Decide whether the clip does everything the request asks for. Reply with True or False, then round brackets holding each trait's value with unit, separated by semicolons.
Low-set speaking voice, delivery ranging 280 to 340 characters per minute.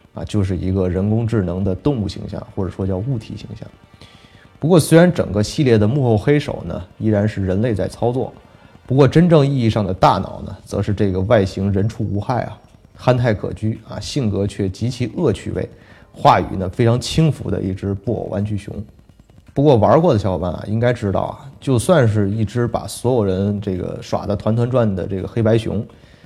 True (105 Hz; 295 characters per minute)